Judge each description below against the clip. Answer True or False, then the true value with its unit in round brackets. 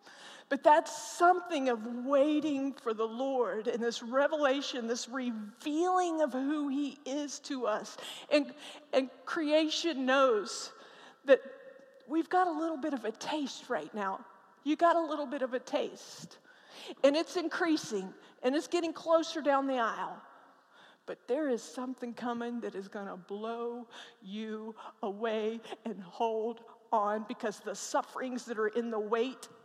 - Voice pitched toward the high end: True (265 Hz)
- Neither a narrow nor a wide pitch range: True (4.6 semitones)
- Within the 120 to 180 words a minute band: True (150 wpm)